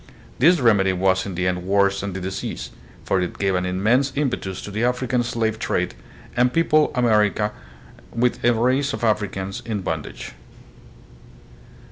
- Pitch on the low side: Yes, low, 105 Hz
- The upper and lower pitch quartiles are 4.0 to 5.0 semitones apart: Yes, average, 4.4 semitones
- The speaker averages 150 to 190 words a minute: Yes, average, 155 wpm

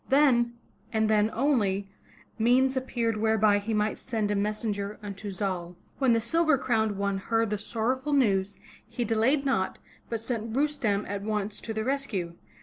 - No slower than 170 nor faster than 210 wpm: No, average, 160 wpm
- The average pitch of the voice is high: Yes, high, 220 Hz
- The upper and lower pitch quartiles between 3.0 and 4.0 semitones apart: Yes, average, 3.5 semitones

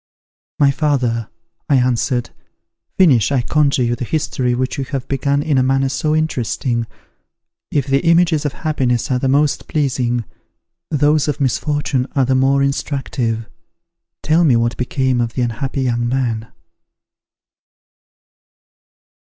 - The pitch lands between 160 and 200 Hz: No, low, 135 Hz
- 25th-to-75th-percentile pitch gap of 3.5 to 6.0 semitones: No, average, 2.9 semitones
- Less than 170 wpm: Yes, slow, 135 wpm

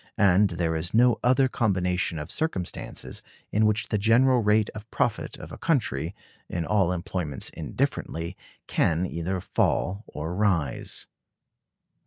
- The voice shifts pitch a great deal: No, average, 4.3 semitones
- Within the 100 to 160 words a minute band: Yes, slow, 135 wpm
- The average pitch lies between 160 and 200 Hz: No, very low, 95 Hz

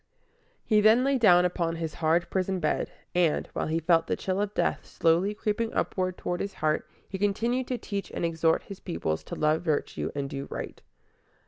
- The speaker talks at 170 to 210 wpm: Yes, average, 195 wpm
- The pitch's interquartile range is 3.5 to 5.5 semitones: Yes, average, 4.0 semitones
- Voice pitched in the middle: Yes, medium, 180 Hz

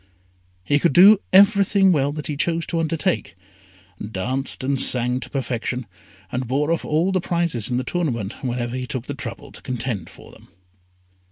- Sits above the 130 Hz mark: Yes, medium, 140 Hz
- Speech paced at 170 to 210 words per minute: Yes, average, 175 wpm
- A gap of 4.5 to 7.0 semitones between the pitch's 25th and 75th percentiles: Yes, average, 5.2 semitones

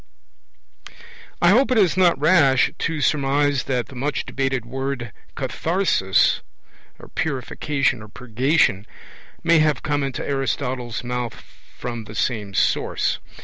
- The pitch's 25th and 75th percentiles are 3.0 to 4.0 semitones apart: Yes, average, 3.6 semitones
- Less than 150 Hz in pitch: Yes, low, 135 Hz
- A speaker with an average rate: No, slow, 120 wpm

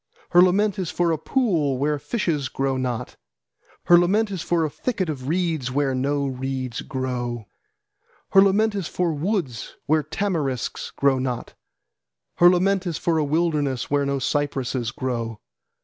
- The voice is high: No, medium, 150 Hz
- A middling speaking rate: Yes, average, 160 wpm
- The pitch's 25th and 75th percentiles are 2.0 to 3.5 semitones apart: No, average, 5.1 semitones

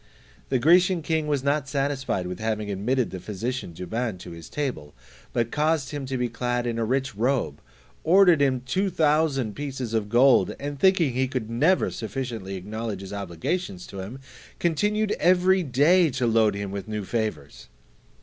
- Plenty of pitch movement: Yes, wide, 5.7 semitones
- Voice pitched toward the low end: Yes, low, 130 Hz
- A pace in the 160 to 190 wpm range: Yes, average, 175 wpm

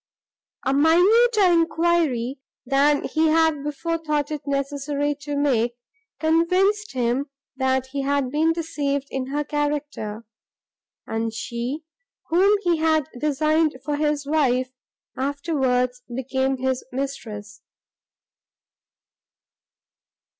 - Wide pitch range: No, average, 3.3 semitones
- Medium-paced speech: No, slow, 105 wpm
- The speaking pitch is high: Yes, very high, 285 Hz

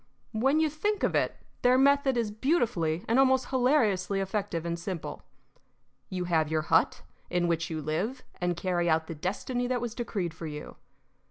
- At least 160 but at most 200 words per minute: Yes, average, 175 wpm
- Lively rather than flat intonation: Yes, wide, 7.1 semitones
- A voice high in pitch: Yes, high, 195 Hz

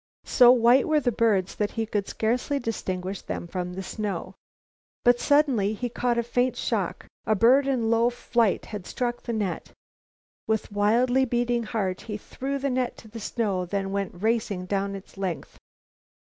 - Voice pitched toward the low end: No, high, 225 Hz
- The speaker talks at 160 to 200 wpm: Yes, average, 175 wpm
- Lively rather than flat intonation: No, average, 3.6 semitones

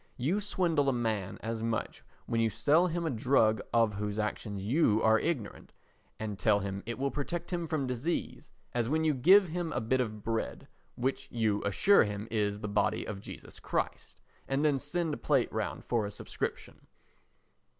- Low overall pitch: Yes, low, 120 Hz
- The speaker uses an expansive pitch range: Yes, wide, 6.2 semitones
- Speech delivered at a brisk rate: No, average, 185 wpm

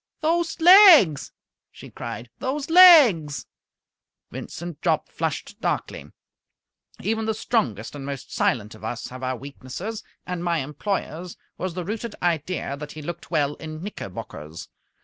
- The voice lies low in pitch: No, medium, 170 Hz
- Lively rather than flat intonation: Yes, wide, 8.0 semitones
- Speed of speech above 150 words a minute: No, slow, 135 wpm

